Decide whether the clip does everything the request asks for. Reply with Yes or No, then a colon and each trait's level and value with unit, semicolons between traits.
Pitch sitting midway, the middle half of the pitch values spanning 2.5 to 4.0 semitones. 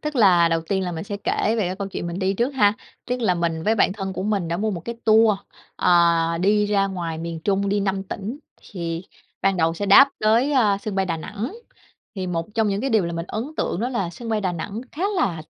No: high, 195 Hz; average, 3.7 semitones